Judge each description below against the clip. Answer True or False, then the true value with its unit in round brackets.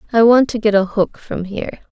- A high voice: True (215 Hz)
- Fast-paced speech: True (250 wpm)